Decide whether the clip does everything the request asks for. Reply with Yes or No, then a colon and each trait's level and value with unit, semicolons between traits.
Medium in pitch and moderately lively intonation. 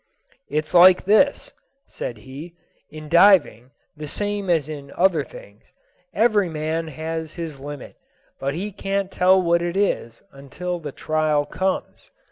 Yes: medium, 165 Hz; average, 4.2 semitones